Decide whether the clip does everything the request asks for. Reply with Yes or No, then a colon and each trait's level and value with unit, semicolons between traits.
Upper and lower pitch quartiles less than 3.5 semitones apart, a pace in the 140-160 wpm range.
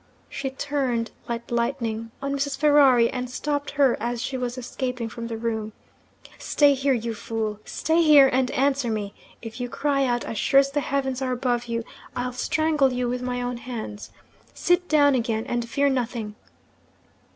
No: average, 3.0 semitones; average, 175 wpm